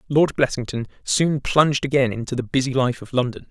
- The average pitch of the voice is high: No, low, 130 Hz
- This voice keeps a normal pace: Yes, average, 190 wpm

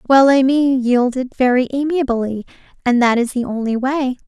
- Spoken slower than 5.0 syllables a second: No, 5.1 syllables/s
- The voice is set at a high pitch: Yes, very high, 255 Hz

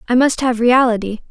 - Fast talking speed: No, average, 185 wpm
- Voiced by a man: No, female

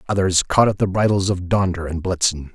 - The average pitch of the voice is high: No, very low, 95 Hz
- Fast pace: Yes, fast, 215 wpm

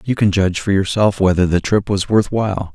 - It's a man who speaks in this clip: Yes, male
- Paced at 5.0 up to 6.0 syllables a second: Yes, 5.7 syllables/s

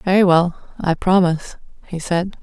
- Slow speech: Yes, slow, 125 wpm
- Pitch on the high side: No, medium, 175 Hz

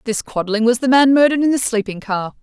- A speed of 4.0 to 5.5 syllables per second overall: No, 6.2 syllables/s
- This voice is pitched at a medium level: No, high, 235 Hz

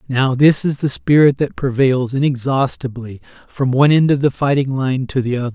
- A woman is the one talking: No, male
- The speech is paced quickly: No, average, 195 wpm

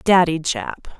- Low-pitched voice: No, medium, 175 Hz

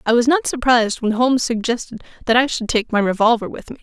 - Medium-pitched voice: No, high, 235 Hz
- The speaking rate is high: Yes, fast, 235 wpm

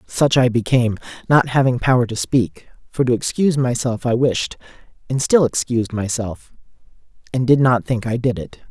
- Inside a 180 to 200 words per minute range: No, average, 170 wpm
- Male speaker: Yes, male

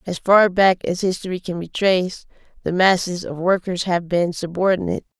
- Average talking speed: Yes, average, 175 wpm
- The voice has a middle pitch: Yes, medium, 180 Hz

